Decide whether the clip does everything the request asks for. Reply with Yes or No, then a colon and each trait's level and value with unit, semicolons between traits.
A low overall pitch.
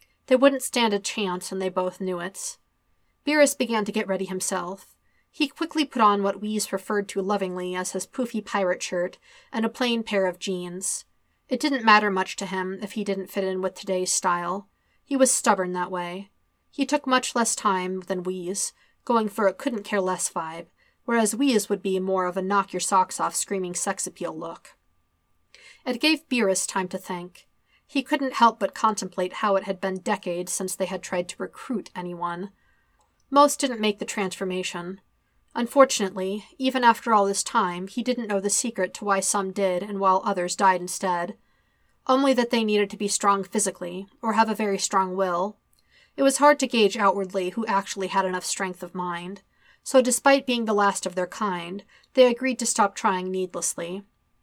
No: high, 195 Hz